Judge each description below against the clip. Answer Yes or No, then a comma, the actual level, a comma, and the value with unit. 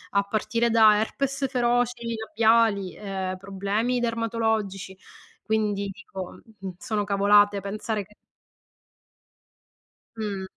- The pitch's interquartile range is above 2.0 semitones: Yes, narrow, 2.5 semitones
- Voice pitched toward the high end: Yes, high, 210 Hz